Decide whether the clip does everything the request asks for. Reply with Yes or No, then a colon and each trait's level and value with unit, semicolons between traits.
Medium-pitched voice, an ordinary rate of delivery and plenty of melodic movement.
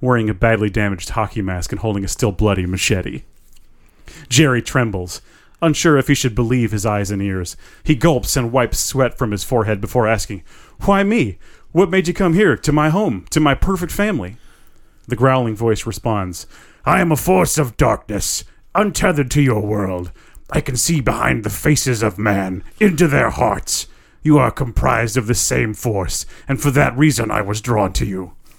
No: low, 115 Hz; average, 185 wpm; wide, 6.7 semitones